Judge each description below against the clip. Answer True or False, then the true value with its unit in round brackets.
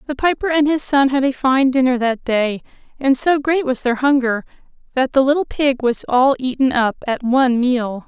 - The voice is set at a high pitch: True (265 Hz)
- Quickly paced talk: True (210 wpm)